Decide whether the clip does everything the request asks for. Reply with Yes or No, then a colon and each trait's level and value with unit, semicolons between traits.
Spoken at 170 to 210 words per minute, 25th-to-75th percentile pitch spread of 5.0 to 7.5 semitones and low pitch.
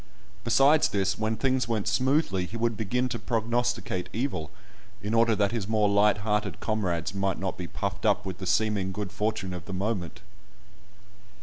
No: average, 175 wpm; average, 3.1 semitones; low, 105 Hz